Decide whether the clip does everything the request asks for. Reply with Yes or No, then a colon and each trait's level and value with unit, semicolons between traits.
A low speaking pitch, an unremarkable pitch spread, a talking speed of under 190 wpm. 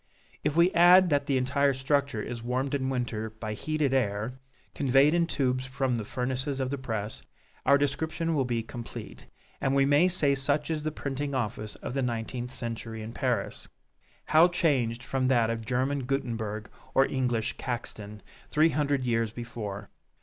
Yes: low, 130 Hz; average, 3.5 semitones; average, 170 wpm